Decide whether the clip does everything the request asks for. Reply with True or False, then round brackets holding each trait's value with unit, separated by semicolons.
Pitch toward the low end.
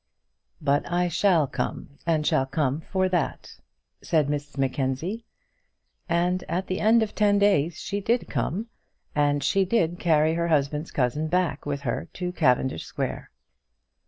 False (160 Hz)